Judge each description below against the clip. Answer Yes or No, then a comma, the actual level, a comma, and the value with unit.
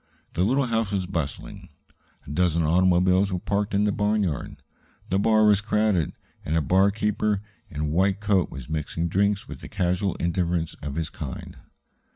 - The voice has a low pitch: Yes, very low, 95 Hz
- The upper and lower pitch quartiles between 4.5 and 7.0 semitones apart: No, average, 3.6 semitones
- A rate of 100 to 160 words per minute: No, average, 170 wpm